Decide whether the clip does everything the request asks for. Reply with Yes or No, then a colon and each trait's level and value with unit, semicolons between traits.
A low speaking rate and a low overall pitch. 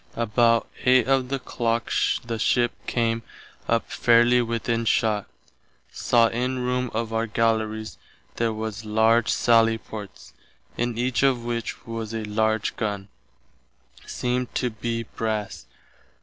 Yes: slow, 130 wpm; low, 115 Hz